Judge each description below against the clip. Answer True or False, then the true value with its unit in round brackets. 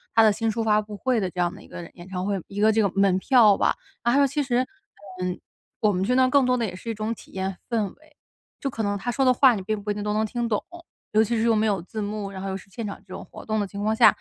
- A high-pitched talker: True (215 Hz)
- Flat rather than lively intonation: False (3.0 semitones)